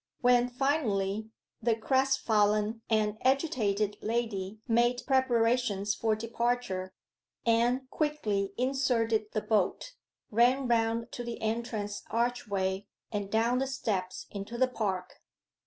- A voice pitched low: No, high, 230 Hz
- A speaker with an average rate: No, slow, 110 wpm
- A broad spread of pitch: No, average, 3.0 semitones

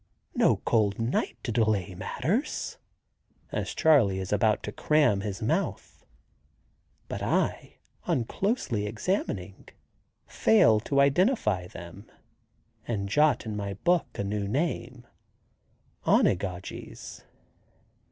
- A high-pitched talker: No, low, 110 Hz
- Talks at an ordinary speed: No, slow, 105 wpm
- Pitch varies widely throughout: Yes, wide, 5.7 semitones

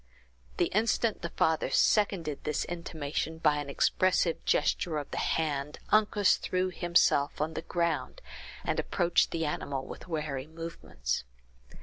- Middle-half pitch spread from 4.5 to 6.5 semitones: No, average, 3.0 semitones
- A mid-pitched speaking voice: Yes, medium, 160 Hz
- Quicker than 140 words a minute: No, slow, 135 wpm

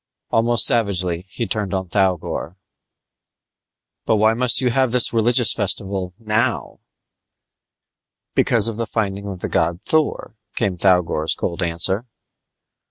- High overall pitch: No, low, 100 Hz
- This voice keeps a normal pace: No, slow, 125 wpm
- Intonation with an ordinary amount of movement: Yes, average, 4.0 semitones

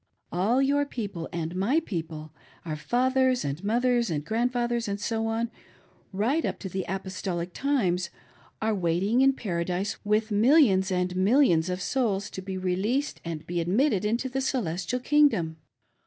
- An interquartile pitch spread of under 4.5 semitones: No, wide, 5.5 semitones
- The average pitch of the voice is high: Yes, high, 205 Hz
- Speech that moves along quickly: No, average, 165 wpm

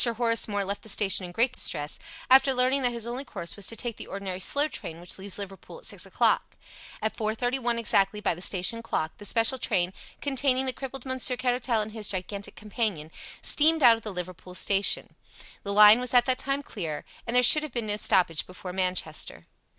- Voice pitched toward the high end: Yes, high, 220 Hz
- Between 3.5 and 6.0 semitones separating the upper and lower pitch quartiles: Yes, average, 4.6 semitones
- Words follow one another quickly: Yes, fast, 210 wpm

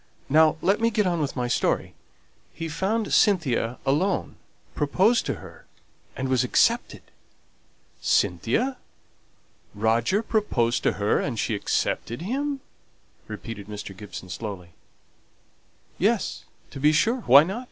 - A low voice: No, medium, 145 Hz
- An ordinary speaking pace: No, slow, 125 wpm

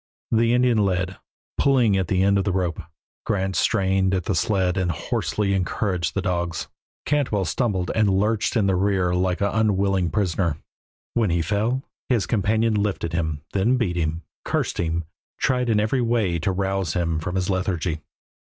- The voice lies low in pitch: Yes, very low, 95 Hz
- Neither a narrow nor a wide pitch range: Yes, average, 3.1 semitones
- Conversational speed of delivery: Yes, average, 170 wpm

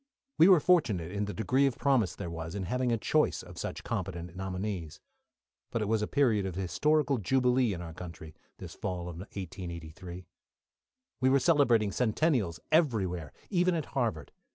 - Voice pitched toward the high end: No, low, 105 Hz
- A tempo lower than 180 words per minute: Yes, average, 170 wpm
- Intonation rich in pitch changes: Yes, wide, 6.9 semitones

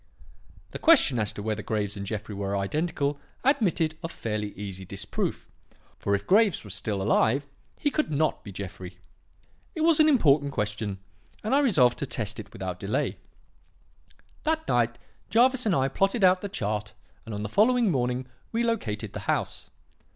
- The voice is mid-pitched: No, low, 125 Hz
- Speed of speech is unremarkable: Yes, average, 170 wpm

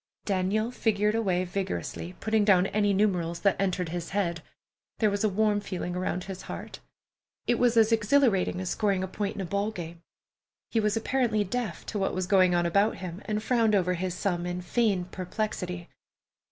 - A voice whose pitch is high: Yes, high, 195 Hz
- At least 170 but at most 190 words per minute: Yes, average, 185 wpm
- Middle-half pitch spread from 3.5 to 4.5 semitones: No, average, 2.9 semitones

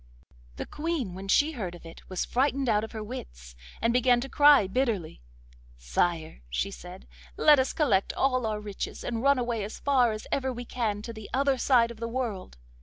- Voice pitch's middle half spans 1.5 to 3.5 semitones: No, average, 5.2 semitones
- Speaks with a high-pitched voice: Yes, high, 230 Hz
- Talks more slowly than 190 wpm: No, average, 200 wpm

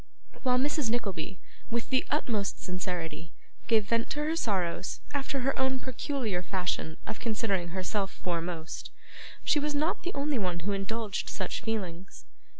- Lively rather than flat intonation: Yes, wide, 6.4 semitones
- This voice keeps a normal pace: Yes, average, 150 wpm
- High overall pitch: Yes, high, 215 Hz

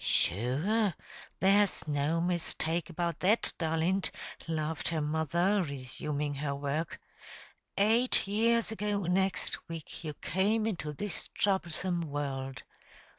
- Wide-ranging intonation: No, average, 4.8 semitones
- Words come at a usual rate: No, slow, 110 wpm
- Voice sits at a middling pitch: Yes, medium, 170 Hz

